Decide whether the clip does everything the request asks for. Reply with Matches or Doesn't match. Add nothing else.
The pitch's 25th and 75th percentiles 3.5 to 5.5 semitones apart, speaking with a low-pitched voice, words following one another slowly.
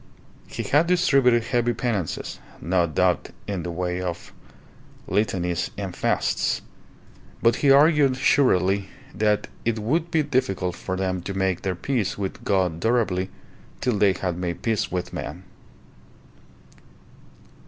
Matches